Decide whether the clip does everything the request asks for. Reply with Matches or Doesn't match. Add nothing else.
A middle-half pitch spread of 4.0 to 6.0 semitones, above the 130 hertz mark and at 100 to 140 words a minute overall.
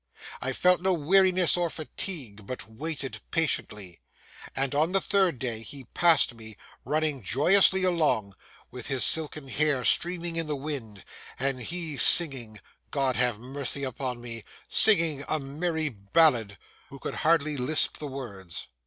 Matches